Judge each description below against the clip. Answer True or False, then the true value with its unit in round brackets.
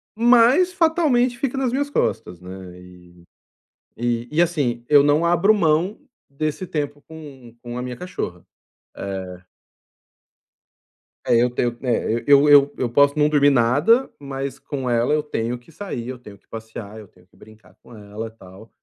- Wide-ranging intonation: True (6.2 semitones)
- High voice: False (135 Hz)